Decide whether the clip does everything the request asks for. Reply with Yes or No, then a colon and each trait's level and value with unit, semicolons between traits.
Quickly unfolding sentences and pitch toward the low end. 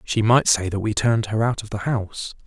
Yes: fast, 270 wpm; low, 110 Hz